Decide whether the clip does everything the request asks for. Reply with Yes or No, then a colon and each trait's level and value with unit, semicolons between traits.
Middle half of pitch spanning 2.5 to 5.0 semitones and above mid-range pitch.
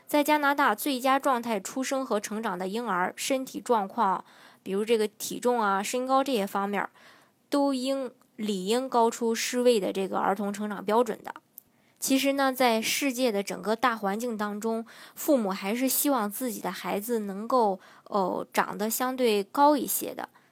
Yes: average, 4.2 semitones; high, 235 Hz